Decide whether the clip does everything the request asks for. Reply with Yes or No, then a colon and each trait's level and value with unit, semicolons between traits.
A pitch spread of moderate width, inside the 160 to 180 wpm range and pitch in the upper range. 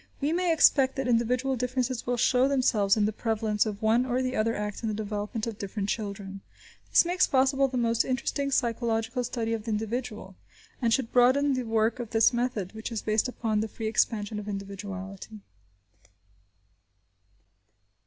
Yes: average, 3.1 semitones; average, 175 wpm; high, 230 Hz